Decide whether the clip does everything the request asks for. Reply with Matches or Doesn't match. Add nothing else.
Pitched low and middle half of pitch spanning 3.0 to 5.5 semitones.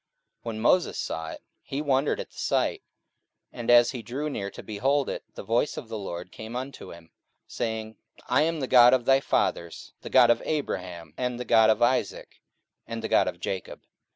Matches